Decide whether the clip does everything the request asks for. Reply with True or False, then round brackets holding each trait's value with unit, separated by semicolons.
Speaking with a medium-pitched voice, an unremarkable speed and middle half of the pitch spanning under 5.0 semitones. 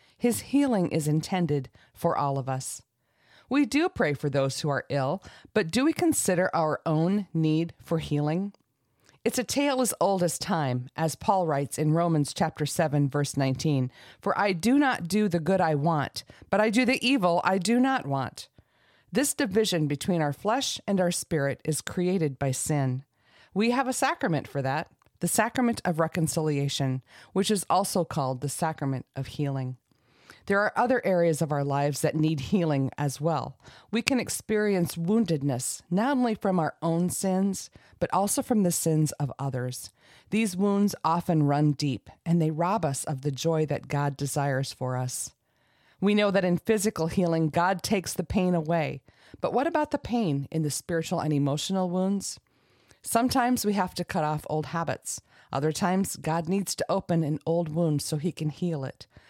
False (165 Hz; 180 wpm; 5.6 semitones)